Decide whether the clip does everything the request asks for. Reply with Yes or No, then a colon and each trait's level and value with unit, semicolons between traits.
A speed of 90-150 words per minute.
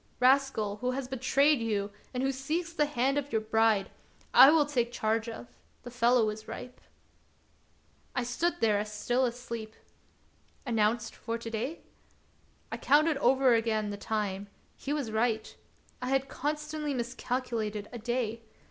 No: average, 160 wpm